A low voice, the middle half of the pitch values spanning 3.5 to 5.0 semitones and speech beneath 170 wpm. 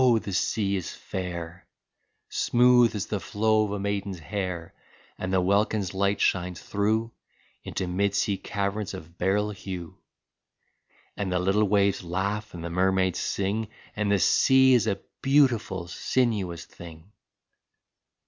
No: low, 100 Hz; narrow, 2.5 semitones; average, 140 wpm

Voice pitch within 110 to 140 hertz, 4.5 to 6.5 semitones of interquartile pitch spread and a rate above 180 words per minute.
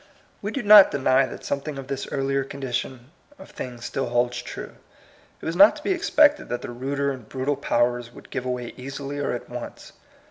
No: low, 135 Hz; average, 2.7 semitones; average, 200 wpm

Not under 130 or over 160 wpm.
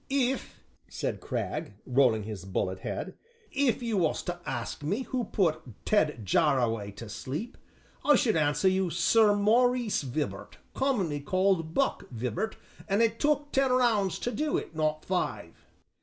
Yes: average, 155 wpm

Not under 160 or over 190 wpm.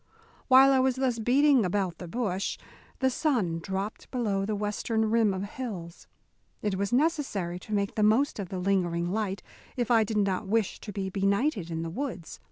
Yes: average, 185 wpm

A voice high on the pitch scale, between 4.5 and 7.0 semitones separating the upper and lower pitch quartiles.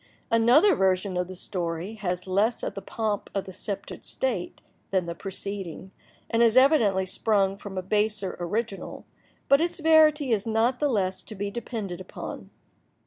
No: high, 205 Hz; average, 3.7 semitones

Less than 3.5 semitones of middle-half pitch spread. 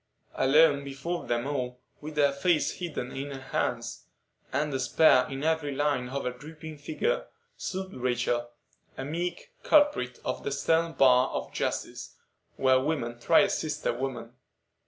No: average, 3.9 semitones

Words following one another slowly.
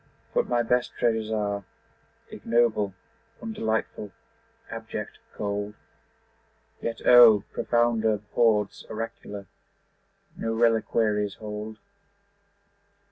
Yes: slow, 80 wpm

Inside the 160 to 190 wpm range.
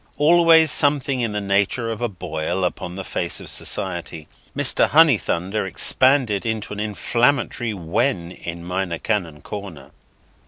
No: slow, 135 wpm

